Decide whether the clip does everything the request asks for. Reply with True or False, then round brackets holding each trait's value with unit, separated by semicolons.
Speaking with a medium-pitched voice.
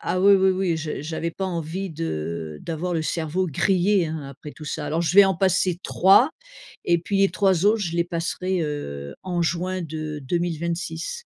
True (170 Hz)